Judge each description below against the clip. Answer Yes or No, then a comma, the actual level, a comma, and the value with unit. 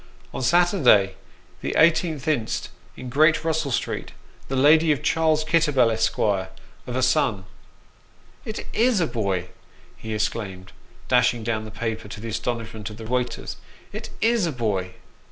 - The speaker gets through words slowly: No, average, 155 wpm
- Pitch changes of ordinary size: No, wide, 6.2 semitones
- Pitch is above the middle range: No, low, 125 Hz